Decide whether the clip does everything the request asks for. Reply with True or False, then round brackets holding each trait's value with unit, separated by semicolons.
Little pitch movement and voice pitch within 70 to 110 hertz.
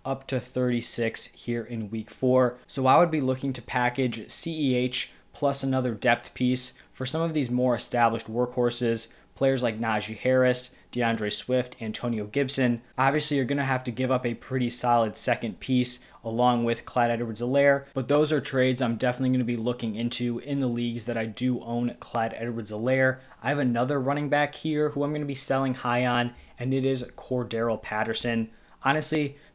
False (2.2 semitones; 125 Hz)